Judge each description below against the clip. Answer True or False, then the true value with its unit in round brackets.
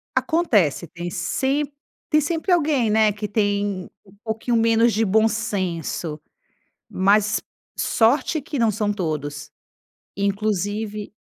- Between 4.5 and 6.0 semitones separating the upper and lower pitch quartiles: False (3.2 semitones)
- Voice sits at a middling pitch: False (210 Hz)